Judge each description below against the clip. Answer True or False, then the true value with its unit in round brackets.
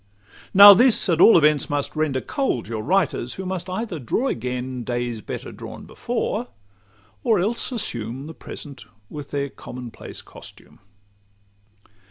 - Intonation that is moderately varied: False (7.2 semitones)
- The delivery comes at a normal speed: True (145 wpm)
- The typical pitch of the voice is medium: True (150 Hz)